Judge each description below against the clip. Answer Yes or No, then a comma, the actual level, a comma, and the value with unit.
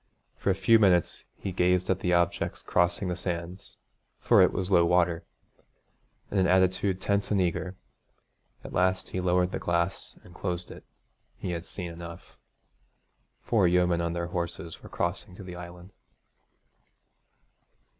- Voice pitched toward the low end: Yes, very low, 90 Hz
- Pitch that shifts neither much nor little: No, narrow, 1.3 semitones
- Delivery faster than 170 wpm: No, average, 155 wpm